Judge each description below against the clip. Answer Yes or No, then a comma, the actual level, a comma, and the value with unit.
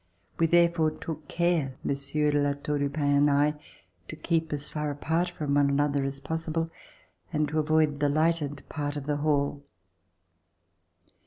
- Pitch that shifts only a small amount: Yes, narrow, 1.9 semitones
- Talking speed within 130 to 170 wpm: Yes, average, 165 wpm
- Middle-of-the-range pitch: Yes, medium, 150 Hz